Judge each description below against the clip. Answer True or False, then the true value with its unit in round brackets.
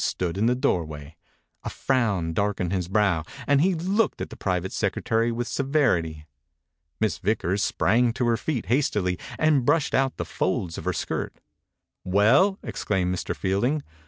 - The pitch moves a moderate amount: False (6.7 semitones)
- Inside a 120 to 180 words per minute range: True (165 wpm)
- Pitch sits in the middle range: False (110 Hz)